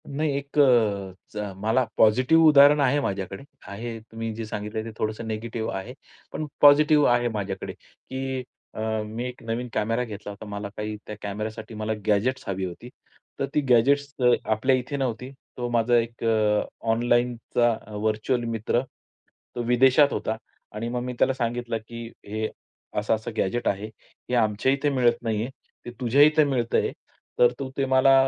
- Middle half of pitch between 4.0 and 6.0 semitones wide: No, average, 3.2 semitones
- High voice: No, low, 115 Hz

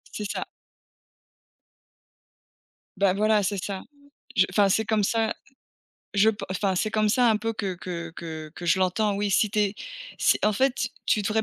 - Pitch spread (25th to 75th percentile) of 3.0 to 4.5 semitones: No, narrow, 2.5 semitones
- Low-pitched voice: No, high, 205 Hz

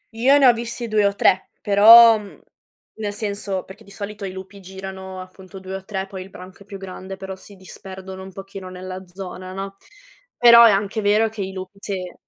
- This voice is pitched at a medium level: No, high, 195 Hz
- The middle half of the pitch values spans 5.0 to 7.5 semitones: No, narrow, 1.8 semitones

